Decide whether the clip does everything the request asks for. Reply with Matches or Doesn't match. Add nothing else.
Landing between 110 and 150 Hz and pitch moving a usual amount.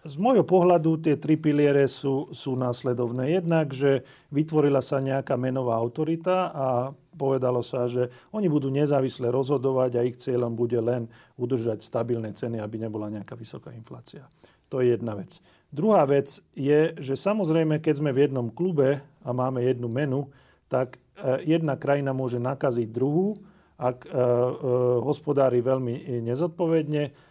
Matches